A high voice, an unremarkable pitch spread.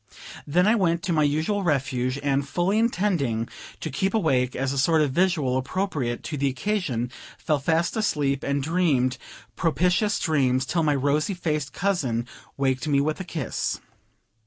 No: medium, 150 Hz; average, 4.9 semitones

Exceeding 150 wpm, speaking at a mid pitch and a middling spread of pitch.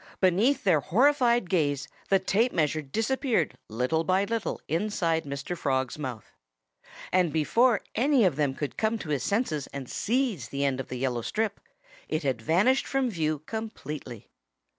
No: average, 160 wpm; medium, 170 Hz; wide, 8.0 semitones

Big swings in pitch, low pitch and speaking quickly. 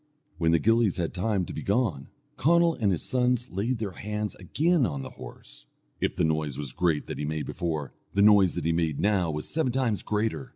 Yes: wide, 6.4 semitones; low, 100 Hz; fast, 215 wpm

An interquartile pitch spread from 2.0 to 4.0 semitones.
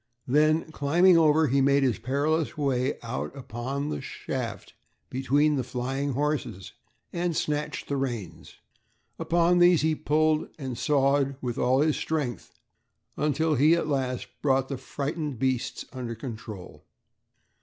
Yes: average, 3.0 semitones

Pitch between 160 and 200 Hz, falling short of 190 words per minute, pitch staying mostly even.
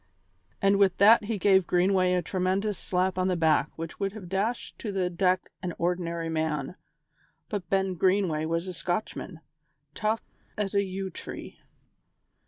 Yes: medium, 185 Hz; average, 160 wpm; narrow, 2.3 semitones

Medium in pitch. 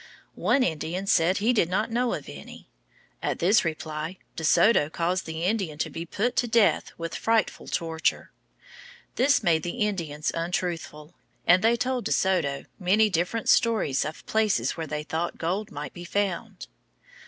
Yes: medium, 180 Hz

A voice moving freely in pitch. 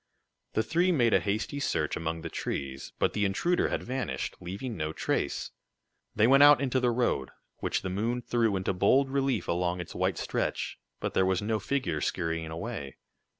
Yes: wide, 6.8 semitones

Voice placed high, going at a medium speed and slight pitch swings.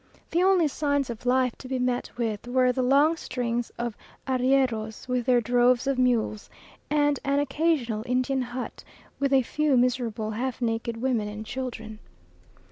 Yes: very high, 250 Hz; average, 160 wpm; narrow, 2.3 semitones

